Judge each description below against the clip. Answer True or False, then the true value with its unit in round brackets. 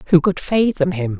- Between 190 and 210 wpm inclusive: True (200 wpm)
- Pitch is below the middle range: False (175 Hz)